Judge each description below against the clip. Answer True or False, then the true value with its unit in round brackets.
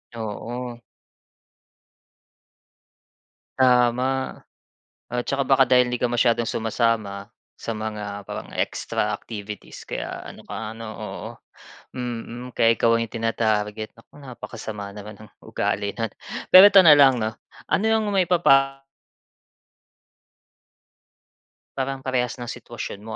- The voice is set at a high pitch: False (120 Hz)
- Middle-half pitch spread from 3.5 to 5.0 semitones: False (3.0 semitones)